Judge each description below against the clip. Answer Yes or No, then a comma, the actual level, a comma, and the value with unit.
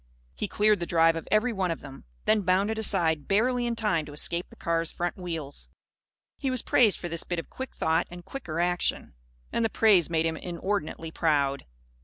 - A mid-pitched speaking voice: Yes, medium, 175 Hz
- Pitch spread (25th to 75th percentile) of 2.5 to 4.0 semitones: No, average, 4.6 semitones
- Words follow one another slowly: No, average, 200 wpm